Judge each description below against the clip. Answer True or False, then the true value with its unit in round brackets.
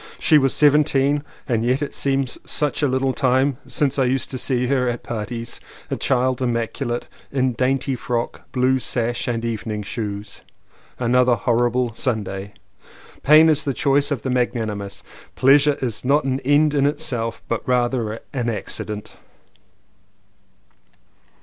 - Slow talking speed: False (150 wpm)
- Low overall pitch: True (125 Hz)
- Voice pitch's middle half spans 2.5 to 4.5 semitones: True (2.8 semitones)